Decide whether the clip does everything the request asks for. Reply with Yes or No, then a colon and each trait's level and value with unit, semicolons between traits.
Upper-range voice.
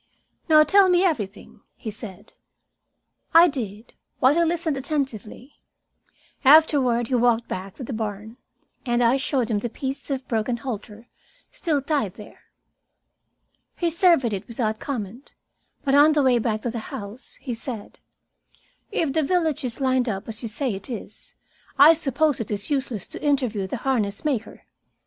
Yes: very high, 250 Hz